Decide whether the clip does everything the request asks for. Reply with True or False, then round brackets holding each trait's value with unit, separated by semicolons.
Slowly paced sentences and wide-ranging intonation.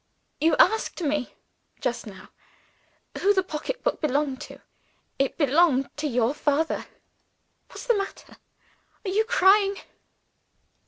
True (115 wpm; 6.3 semitones)